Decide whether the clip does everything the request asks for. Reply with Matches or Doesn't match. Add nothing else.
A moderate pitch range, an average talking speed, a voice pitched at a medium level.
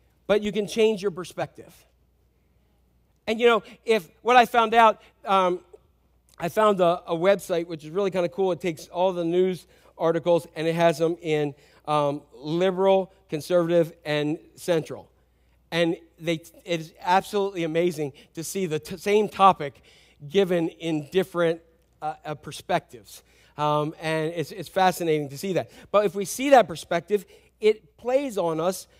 Matches